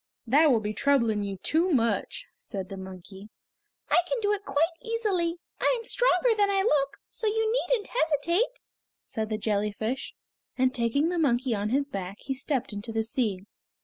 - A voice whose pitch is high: Yes, very high, 275 Hz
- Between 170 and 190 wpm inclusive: Yes, average, 180 wpm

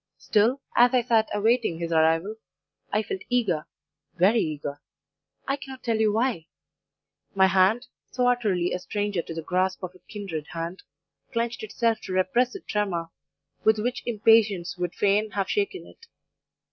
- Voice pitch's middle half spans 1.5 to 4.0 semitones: No, average, 4.6 semitones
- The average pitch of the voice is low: No, high, 205 Hz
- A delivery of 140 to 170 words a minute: Yes, average, 160 wpm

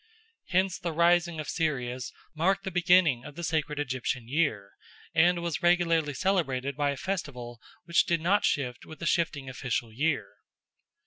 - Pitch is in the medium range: Yes, medium, 155 Hz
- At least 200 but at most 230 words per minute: No, average, 155 wpm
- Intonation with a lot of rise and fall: No, average, 4.6 semitones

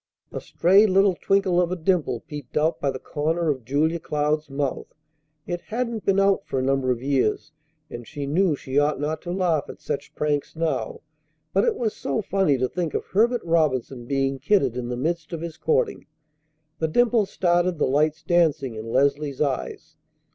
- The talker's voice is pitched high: No, medium, 155 Hz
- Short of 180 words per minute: No, average, 190 wpm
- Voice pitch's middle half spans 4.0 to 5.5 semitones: Yes, average, 4.8 semitones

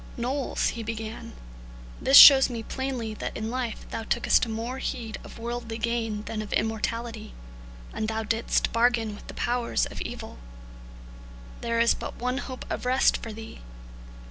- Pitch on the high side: Yes, high, 230 Hz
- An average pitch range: No, narrow, 1.8 semitones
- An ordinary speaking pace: Yes, average, 160 wpm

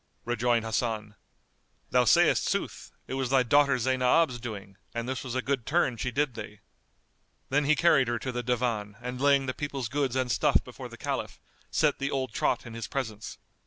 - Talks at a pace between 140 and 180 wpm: No, average, 195 wpm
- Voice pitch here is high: No, low, 125 Hz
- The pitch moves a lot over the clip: No, average, 2.9 semitones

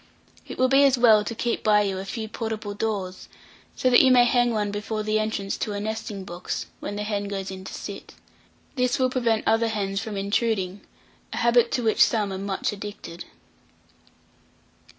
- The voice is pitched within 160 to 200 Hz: No, high, 215 Hz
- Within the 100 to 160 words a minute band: No, average, 190 wpm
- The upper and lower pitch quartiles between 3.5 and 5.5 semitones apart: No, narrow, 2.5 semitones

